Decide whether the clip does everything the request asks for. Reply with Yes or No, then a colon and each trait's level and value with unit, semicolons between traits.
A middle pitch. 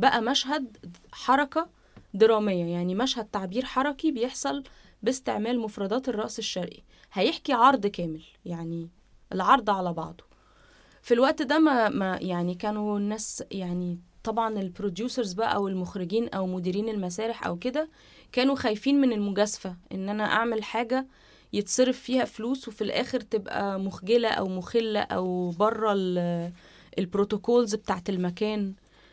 No: high, 215 Hz